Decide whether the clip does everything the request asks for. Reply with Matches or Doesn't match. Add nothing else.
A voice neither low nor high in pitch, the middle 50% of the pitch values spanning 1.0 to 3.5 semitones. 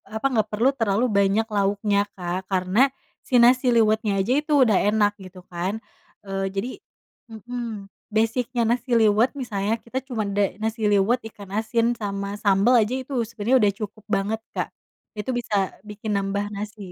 Doesn't match